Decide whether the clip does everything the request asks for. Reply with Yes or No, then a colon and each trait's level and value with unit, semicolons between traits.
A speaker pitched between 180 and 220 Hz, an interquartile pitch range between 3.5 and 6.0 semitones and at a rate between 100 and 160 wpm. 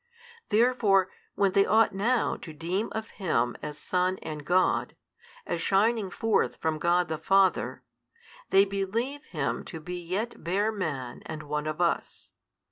Yes: medium, 185 Hz; average, 4.5 semitones; average, 150 wpm